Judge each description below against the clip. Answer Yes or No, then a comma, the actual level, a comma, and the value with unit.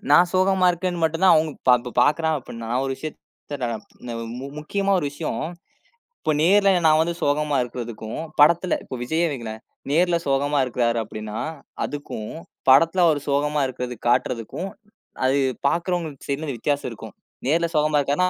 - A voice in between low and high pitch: Yes, medium, 150 Hz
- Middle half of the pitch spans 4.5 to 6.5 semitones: Yes, average, 4.8 semitones